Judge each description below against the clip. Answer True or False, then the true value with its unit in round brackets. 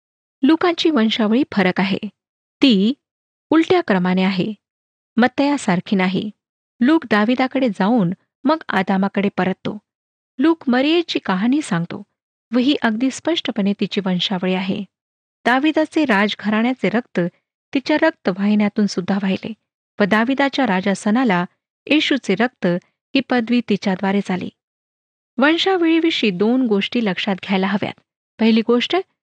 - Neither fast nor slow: True (110 wpm)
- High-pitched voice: True (220 Hz)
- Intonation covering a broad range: True (5.7 semitones)